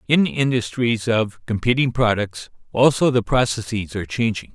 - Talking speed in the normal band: No, slow, 130 wpm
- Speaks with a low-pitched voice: Yes, low, 115 Hz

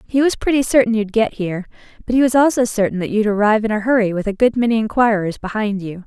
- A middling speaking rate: No, fast, 245 wpm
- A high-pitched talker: Yes, high, 220 Hz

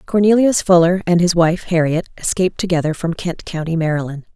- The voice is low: No, medium, 175 Hz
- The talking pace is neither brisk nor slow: Yes, average, 165 wpm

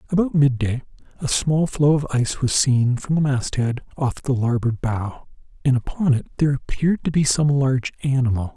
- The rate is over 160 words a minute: Yes, average, 180 wpm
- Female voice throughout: No, male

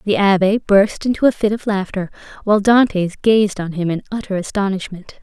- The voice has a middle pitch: No, high, 200 Hz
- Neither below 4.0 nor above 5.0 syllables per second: No, 5.4 syllables/s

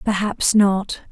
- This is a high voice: Yes, high, 200 Hz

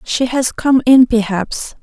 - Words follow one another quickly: No, average, 165 wpm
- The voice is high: Yes, high, 245 Hz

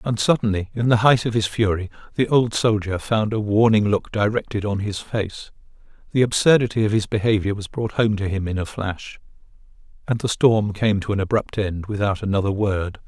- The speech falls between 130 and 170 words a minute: No, average, 195 wpm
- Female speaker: No, male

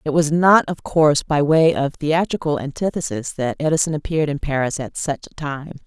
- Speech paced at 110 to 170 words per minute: No, average, 195 wpm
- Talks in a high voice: No, medium, 150 Hz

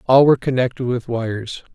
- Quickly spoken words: No, average, 170 wpm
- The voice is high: No, low, 125 Hz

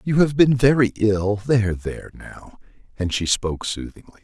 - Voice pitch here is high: No, low, 110 Hz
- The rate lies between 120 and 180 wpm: Yes, average, 170 wpm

